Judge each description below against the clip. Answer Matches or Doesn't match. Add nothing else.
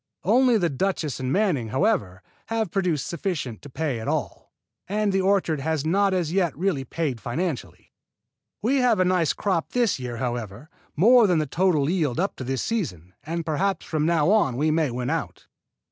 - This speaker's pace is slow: Doesn't match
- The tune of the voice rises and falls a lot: Matches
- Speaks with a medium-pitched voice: Matches